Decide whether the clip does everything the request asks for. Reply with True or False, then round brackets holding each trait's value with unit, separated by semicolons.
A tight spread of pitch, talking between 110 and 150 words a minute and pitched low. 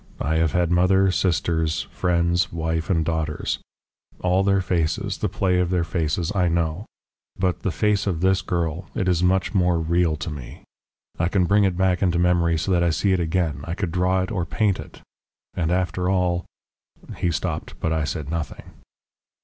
False (2.2 semitones; 190 wpm; 90 Hz)